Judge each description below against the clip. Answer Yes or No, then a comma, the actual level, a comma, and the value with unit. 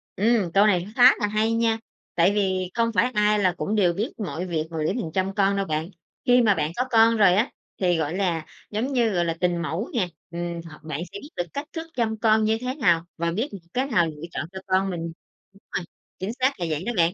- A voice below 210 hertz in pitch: Yes, high, 195 Hz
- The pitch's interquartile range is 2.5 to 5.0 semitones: Yes, average, 4.6 semitones